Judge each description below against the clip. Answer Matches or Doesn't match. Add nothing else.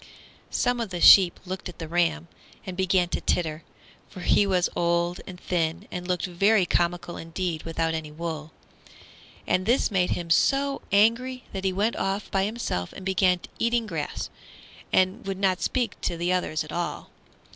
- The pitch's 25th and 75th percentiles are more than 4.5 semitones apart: Doesn't match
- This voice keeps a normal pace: Matches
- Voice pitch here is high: Doesn't match